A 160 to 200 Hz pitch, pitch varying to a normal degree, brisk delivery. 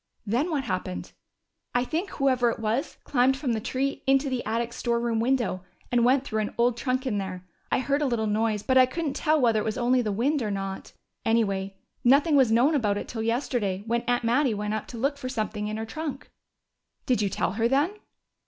No: high, 240 Hz; average, 3.6 semitones; fast, 220 wpm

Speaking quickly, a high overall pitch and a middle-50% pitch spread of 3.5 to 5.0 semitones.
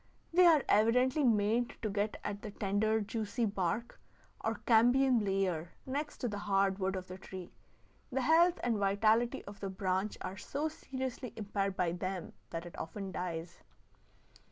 No: average, 160 wpm; high, 205 Hz; average, 4.0 semitones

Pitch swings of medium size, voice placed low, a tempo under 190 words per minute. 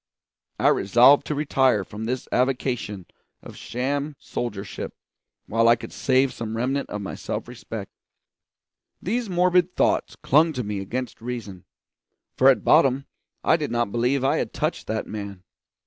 Yes: average, 4.2 semitones; low, 125 Hz; average, 150 wpm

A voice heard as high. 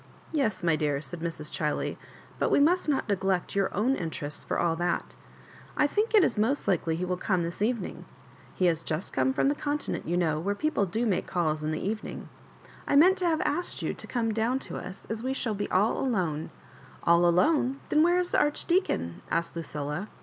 Yes: high, 195 Hz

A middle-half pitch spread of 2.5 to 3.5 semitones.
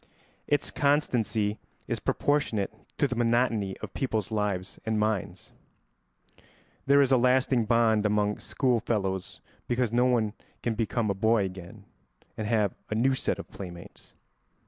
Yes: average, 3.1 semitones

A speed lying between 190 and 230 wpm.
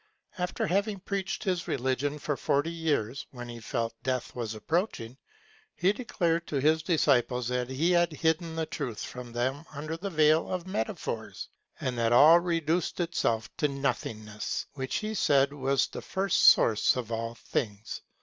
No: average, 160 wpm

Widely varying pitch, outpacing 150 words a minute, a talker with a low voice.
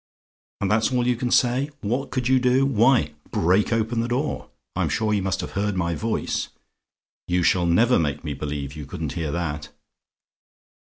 Yes: wide, 6.5 semitones; average, 180 wpm; low, 105 Hz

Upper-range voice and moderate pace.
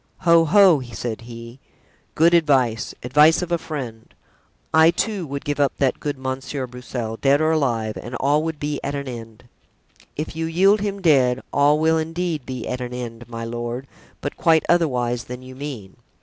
No: medium, 140 Hz; average, 180 wpm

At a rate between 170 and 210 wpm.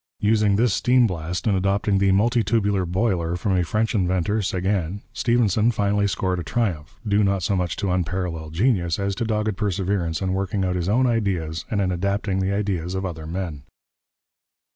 Yes: average, 180 wpm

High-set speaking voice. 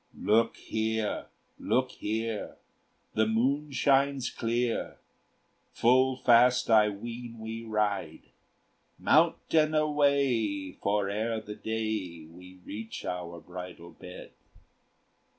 No: low, 110 Hz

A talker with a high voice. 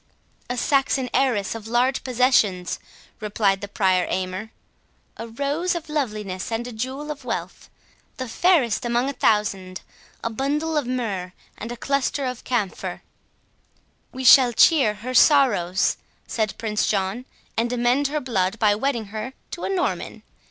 Yes: high, 240 Hz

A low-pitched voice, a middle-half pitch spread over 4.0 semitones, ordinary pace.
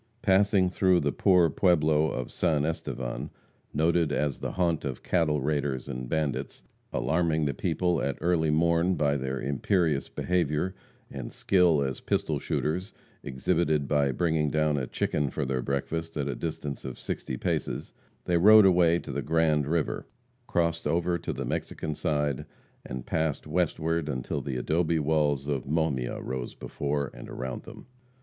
No: very low, 75 Hz; average, 3.2 semitones; average, 155 wpm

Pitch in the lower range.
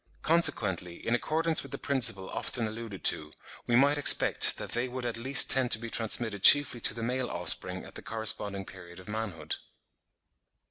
Yes: low, 115 Hz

